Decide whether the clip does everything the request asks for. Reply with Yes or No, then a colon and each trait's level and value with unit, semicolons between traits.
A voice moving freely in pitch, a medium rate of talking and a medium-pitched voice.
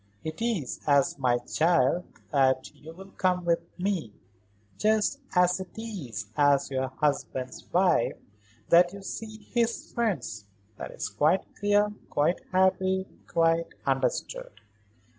No: wide, 5.9 semitones; slow, 125 wpm; medium, 170 Hz